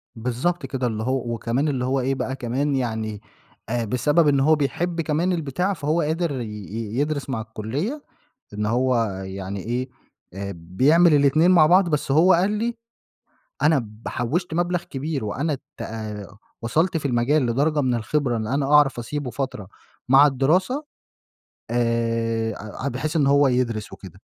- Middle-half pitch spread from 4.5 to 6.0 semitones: Yes, average, 4.8 semitones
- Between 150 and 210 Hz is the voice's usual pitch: No, low, 135 Hz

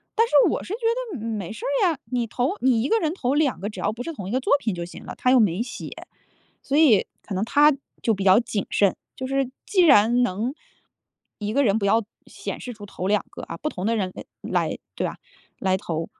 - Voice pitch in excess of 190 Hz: Yes, high, 230 Hz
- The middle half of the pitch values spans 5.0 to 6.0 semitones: Yes, wide, 5.6 semitones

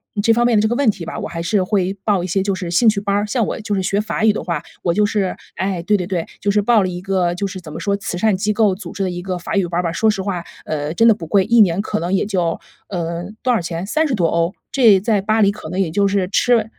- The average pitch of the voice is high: Yes, high, 195 Hz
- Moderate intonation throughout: Yes, average, 3.2 semitones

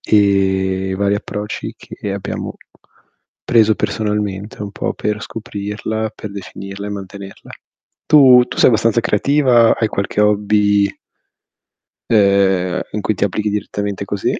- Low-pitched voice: Yes, low, 105 Hz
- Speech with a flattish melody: Yes, narrow, 1.3 semitones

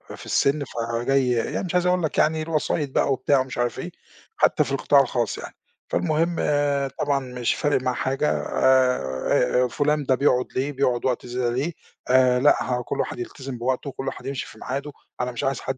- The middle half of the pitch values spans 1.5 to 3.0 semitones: Yes, average, 2.7 semitones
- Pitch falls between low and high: No, low, 130 Hz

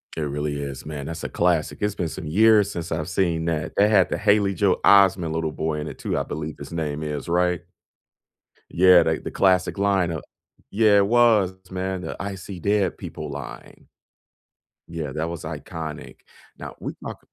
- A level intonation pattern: No, average, 3.9 semitones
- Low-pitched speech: Yes, very low, 85 Hz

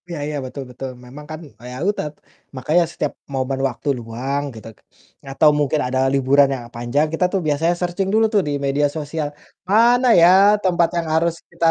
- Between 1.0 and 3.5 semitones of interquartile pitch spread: No, average, 4.2 semitones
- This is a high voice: No, medium, 150 Hz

